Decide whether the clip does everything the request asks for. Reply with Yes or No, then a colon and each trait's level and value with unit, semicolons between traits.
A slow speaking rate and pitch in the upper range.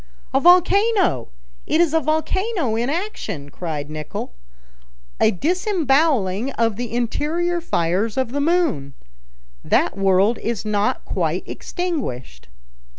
Yes: slow, 115 wpm; very high, 260 Hz